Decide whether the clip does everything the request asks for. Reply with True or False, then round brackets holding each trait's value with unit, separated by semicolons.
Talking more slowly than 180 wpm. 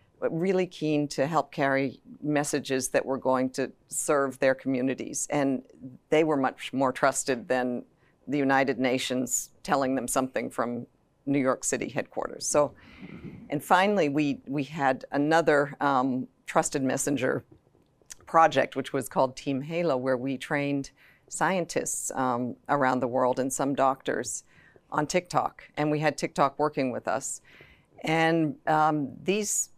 True (140 wpm)